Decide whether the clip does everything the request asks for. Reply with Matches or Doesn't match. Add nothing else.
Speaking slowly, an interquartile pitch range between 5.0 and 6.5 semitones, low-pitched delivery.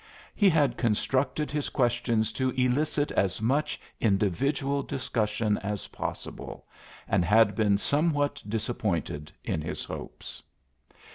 Matches